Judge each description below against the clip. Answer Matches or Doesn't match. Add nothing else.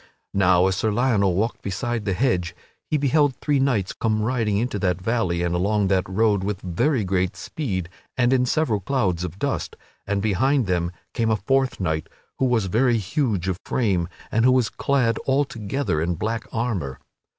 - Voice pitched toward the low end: Matches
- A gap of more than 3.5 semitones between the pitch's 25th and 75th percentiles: Matches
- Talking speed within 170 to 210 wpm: Matches